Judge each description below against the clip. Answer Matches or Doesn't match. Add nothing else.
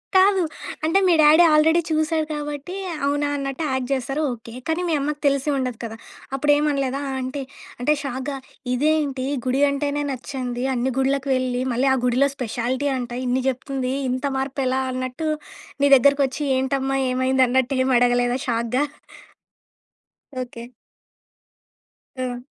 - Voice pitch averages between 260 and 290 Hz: Matches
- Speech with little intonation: Matches